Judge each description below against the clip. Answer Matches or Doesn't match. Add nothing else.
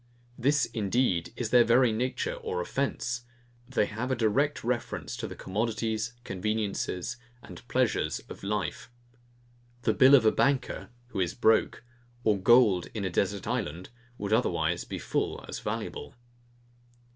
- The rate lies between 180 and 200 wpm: Doesn't match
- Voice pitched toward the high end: Doesn't match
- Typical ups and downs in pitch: Matches